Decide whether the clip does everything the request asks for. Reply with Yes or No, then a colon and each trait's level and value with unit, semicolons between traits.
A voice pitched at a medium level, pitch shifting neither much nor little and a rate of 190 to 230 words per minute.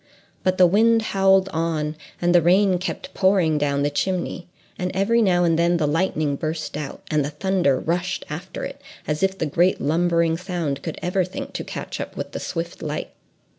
Yes: medium, 175 Hz; average, 3.3 semitones; average, 195 wpm